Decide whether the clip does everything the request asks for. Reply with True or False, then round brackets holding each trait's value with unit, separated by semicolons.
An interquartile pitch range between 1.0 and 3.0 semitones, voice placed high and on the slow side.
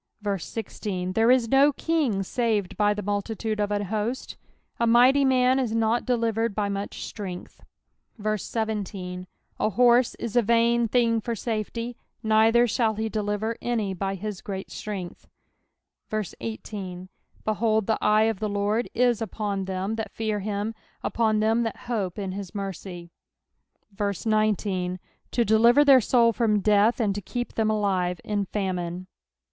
False (2.6 semitones; 215 Hz; 150 wpm)